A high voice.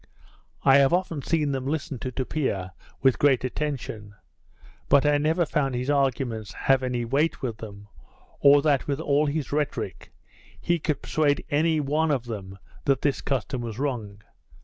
No: medium, 140 Hz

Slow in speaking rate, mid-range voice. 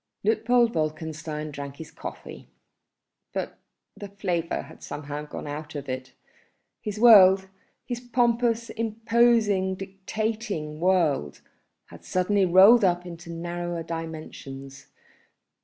Yes: slow, 105 wpm; medium, 180 Hz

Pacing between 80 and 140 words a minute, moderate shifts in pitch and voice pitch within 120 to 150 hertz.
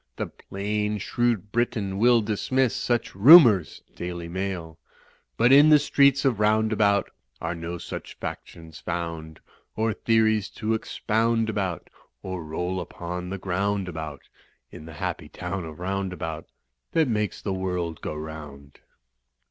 No: slow, 135 wpm; average, 4.6 semitones; very low, 95 Hz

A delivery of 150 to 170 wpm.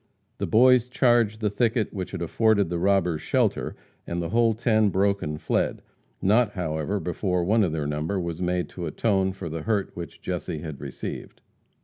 No: average, 185 wpm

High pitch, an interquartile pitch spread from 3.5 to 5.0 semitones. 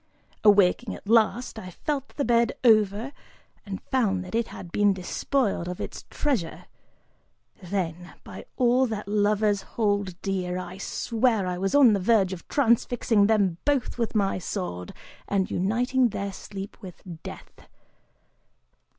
Yes: high, 205 Hz; average, 3.8 semitones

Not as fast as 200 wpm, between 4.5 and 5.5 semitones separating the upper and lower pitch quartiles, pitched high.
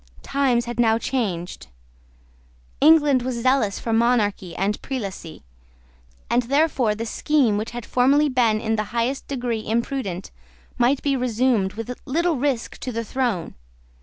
No: average, 140 wpm; average, 3.4 semitones; high, 240 Hz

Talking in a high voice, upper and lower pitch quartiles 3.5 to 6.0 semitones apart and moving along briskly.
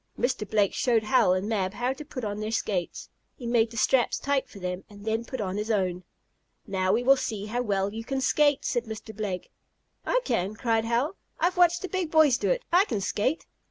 Yes: high, 225 Hz; average, 4.6 semitones; fast, 225 wpm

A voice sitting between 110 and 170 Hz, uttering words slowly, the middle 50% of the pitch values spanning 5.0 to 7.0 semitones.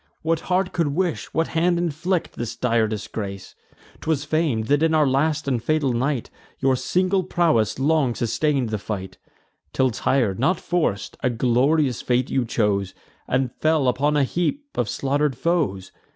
No: medium, 140 Hz; average, 160 wpm; average, 5.3 semitones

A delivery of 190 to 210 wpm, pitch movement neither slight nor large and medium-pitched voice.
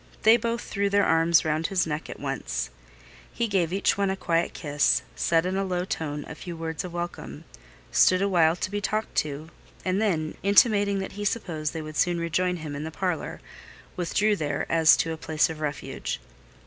Yes: average, 200 wpm; average, 3.8 semitones; medium, 170 Hz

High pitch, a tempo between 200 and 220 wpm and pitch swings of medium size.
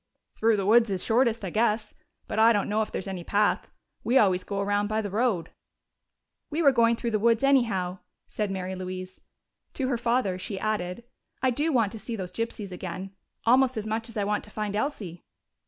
Yes: high, 215 Hz; fast, 205 wpm; average, 3.3 semitones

